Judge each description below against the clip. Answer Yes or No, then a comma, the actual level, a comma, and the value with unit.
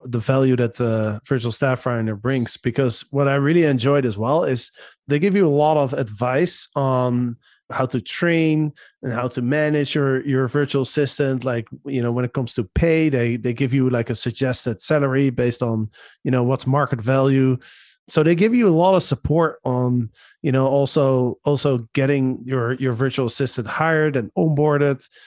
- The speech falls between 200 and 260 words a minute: No, average, 190 wpm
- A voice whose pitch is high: No, low, 135 Hz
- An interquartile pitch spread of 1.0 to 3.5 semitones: Yes, average, 2.7 semitones